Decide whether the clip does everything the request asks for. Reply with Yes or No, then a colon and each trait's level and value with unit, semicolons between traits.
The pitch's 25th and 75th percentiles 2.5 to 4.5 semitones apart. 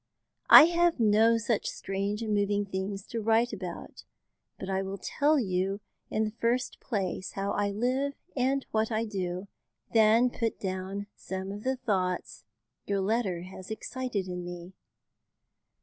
Yes: average, 3.3 semitones